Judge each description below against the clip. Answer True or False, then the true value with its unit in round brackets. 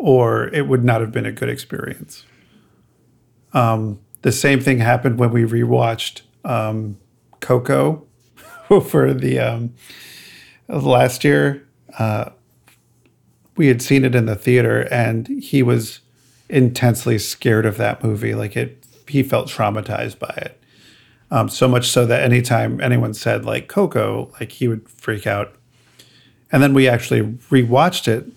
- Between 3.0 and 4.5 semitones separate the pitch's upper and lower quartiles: False (2.5 semitones)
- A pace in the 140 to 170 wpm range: True (145 wpm)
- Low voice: True (120 Hz)